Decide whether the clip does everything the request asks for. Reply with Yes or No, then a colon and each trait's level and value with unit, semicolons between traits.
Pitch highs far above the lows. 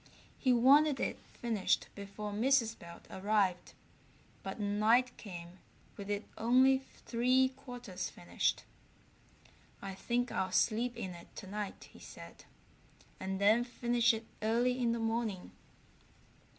No: average, 3.7 semitones